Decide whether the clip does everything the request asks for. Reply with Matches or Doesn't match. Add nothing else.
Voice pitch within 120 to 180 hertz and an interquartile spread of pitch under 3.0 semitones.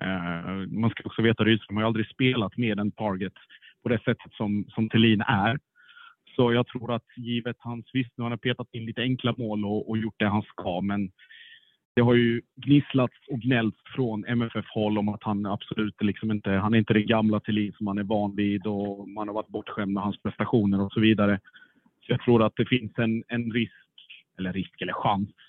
Doesn't match